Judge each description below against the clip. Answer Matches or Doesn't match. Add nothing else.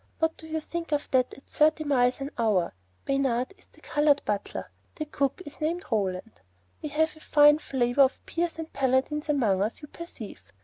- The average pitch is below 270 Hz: Doesn't match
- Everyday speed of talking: Matches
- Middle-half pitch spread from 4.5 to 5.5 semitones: Doesn't match